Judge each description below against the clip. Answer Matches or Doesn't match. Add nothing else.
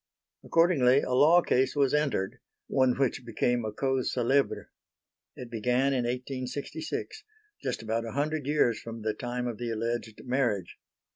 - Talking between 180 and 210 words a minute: Doesn't match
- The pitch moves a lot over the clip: Doesn't match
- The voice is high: Doesn't match